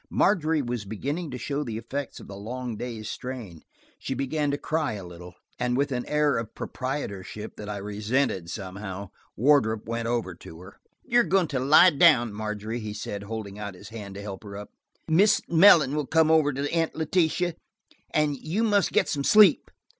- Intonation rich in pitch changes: Yes, wide, 6.4 semitones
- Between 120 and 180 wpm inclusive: No, average, 190 wpm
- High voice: No, low, 125 Hz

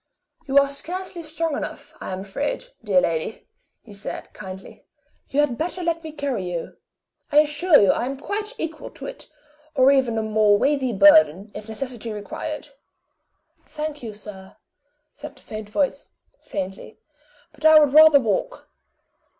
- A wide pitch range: Yes, wide, 6.7 semitones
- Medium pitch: No, very high, 270 Hz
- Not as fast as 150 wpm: No, average, 160 wpm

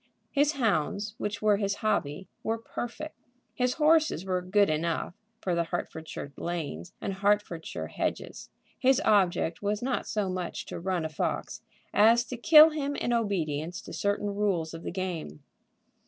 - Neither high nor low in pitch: No, high, 200 Hz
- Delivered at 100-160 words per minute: Yes, average, 155 wpm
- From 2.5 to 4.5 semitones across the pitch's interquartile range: No, average, 5.1 semitones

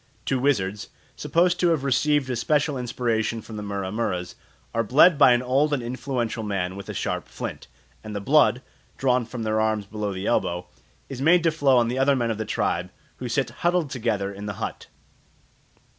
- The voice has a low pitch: Yes, low, 120 Hz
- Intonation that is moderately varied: Yes, average, 4.6 semitones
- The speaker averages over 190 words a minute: Yes, average, 200 wpm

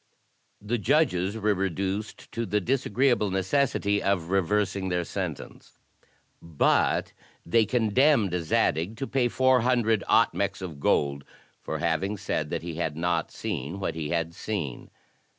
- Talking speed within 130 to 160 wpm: Yes, slow, 135 wpm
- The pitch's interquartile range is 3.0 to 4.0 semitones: No, average, 4.8 semitones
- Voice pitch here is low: Yes, low, 100 Hz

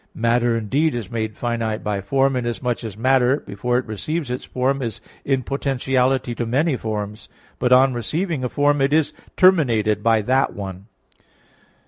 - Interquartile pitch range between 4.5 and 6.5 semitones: No, average, 3.3 semitones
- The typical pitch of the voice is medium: No, low, 125 Hz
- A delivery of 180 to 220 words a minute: No, average, 160 wpm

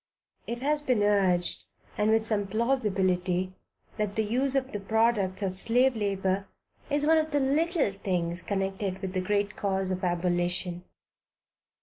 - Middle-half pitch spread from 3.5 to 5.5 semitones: Yes, average, 4.1 semitones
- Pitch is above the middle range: Yes, high, 200 Hz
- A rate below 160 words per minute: Yes, average, 150 wpm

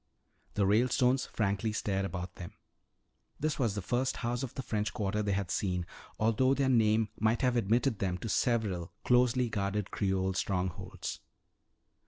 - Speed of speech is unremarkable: Yes, average, 155 wpm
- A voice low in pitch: Yes, low, 105 Hz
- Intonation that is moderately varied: Yes, average, 3.9 semitones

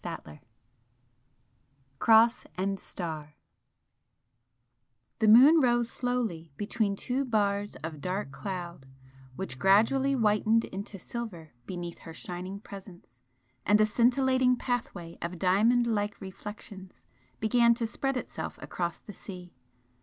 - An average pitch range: Yes, average, 4.7 semitones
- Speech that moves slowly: Yes, slow, 115 wpm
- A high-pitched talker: Yes, high, 205 Hz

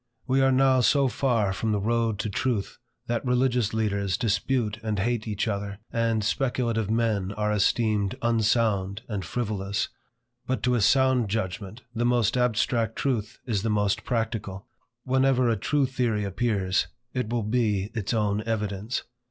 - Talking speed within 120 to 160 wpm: Yes, average, 155 wpm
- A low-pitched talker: Yes, low, 110 Hz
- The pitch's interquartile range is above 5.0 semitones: No, average, 3.1 semitones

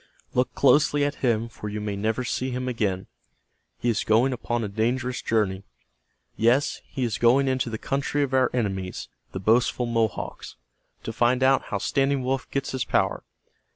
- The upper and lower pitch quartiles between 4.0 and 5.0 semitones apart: No, average, 3.2 semitones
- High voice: No, low, 120 Hz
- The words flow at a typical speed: Yes, average, 175 wpm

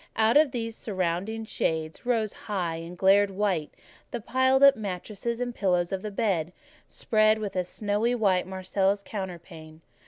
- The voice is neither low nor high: No, high, 200 Hz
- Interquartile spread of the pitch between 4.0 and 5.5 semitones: No, average, 3.6 semitones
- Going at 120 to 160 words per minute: Yes, average, 155 wpm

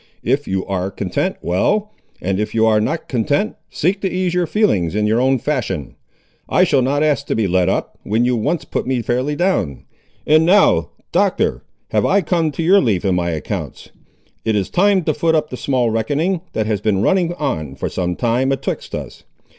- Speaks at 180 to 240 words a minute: Yes, average, 200 wpm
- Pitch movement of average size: No, wide, 7.9 semitones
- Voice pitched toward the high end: No, low, 130 Hz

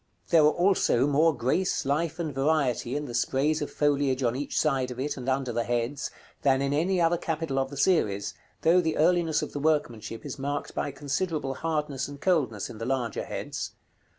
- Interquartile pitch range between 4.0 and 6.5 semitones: No, average, 3.3 semitones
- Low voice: No, medium, 145 Hz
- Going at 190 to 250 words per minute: Yes, average, 200 wpm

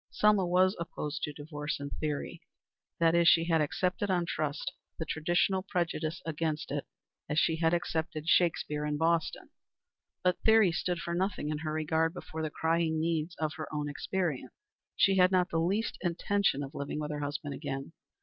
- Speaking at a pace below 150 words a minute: No, average, 180 wpm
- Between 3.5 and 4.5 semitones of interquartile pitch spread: No, average, 2.7 semitones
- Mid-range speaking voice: Yes, medium, 165 Hz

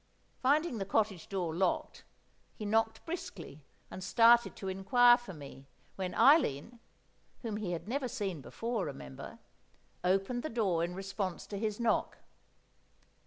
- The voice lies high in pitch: Yes, high, 205 Hz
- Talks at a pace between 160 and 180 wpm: No, average, 140 wpm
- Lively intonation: No, average, 4.7 semitones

